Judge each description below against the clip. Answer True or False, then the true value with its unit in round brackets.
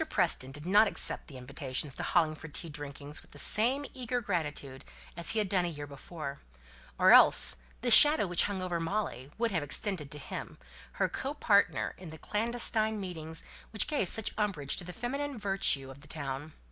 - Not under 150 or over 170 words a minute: False (190 wpm)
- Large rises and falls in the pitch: True (6.5 semitones)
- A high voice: False (175 Hz)